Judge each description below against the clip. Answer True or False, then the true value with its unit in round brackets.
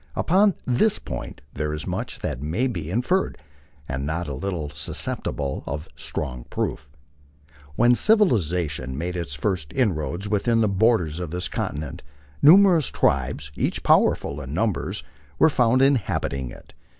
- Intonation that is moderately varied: False (8.6 semitones)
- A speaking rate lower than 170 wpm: True (140 wpm)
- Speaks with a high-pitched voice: False (90 Hz)